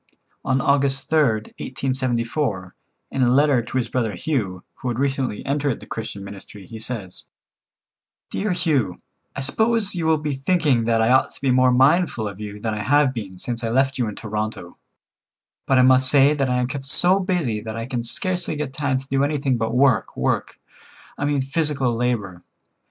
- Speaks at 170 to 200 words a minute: Yes, average, 190 wpm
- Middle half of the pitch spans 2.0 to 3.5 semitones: No, average, 4.0 semitones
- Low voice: Yes, low, 130 Hz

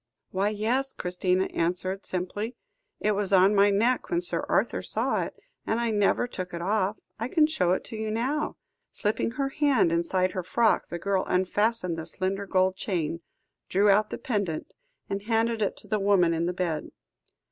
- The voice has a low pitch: No, high, 200 Hz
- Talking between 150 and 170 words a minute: No, average, 185 wpm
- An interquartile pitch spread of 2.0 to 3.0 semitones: No, average, 3.4 semitones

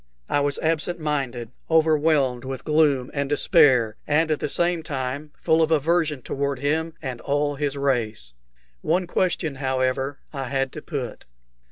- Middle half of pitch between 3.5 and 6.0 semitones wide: No, average, 3.1 semitones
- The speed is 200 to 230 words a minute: No, average, 155 wpm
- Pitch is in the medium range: Yes, medium, 145 Hz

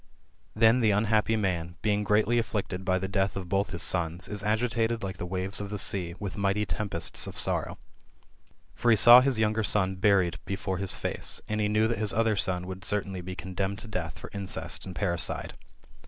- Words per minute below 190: No, fast, 205 wpm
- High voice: No, low, 100 Hz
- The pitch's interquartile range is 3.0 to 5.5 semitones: No, narrow, 2.5 semitones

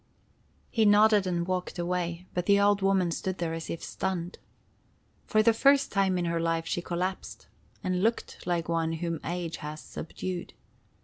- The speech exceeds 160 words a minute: Yes, average, 170 wpm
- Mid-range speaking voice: Yes, medium, 180 Hz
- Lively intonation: No, narrow, 2.6 semitones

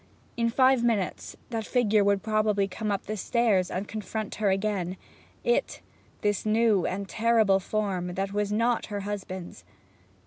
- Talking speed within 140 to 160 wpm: Yes, average, 150 wpm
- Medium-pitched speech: No, high, 210 Hz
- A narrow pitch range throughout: Yes, narrow, 2.2 semitones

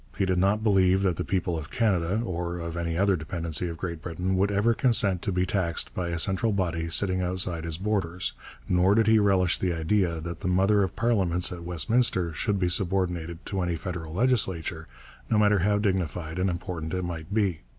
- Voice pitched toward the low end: Yes, very low, 90 Hz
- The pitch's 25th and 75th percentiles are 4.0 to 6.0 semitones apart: No, average, 2.7 semitones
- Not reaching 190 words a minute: No, average, 200 wpm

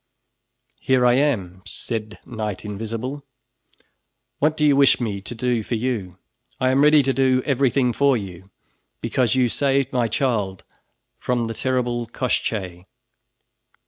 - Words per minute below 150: Yes, average, 140 wpm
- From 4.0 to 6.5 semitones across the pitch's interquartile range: No, average, 3.6 semitones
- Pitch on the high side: No, low, 125 Hz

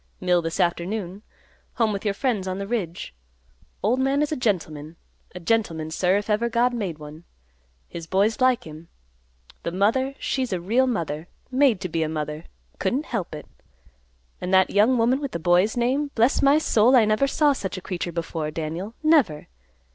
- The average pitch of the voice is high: Yes, high, 200 Hz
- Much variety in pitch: Yes, wide, 6.4 semitones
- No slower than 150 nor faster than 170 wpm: No, average, 185 wpm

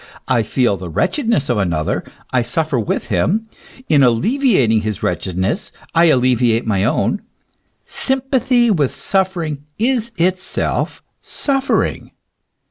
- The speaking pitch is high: No, medium, 145 Hz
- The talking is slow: Yes, slow, 115 wpm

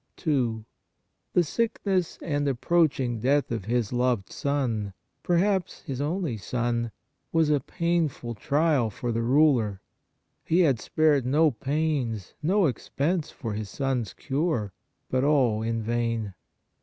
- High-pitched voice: No, low, 135 Hz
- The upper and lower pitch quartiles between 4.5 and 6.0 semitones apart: Yes, average, 5.2 semitones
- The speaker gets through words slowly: Yes, slow, 130 wpm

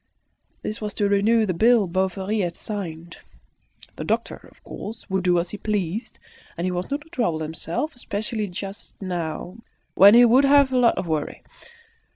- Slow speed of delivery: No, average, 175 wpm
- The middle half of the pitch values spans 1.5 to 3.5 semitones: No, average, 4.4 semitones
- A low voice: No, high, 200 Hz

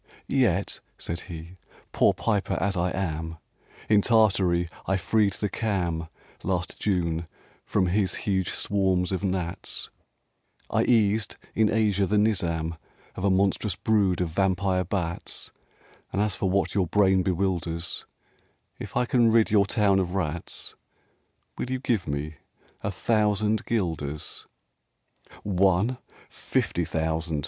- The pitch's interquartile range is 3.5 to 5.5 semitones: No, average, 3.1 semitones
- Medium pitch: No, very low, 95 Hz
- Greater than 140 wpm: No, slow, 135 wpm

